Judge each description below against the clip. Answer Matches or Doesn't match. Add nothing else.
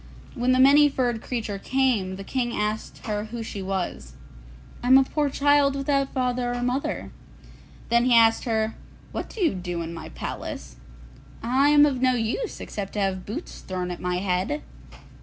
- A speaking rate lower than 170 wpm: Doesn't match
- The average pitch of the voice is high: Matches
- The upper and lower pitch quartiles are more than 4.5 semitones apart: Matches